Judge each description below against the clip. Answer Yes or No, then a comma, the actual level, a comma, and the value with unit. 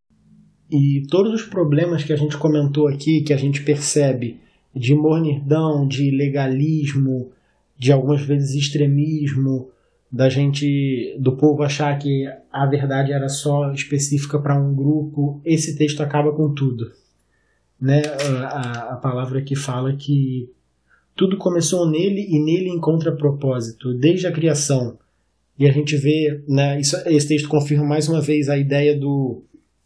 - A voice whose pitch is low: No, medium, 145 Hz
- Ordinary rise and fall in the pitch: No, narrow, 1.9 semitones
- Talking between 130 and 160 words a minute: Yes, average, 145 wpm